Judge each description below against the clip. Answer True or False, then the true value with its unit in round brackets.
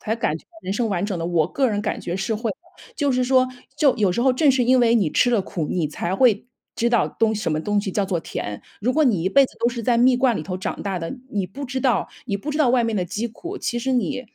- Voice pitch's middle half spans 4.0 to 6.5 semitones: True (4.9 semitones)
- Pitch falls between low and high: False (225 Hz)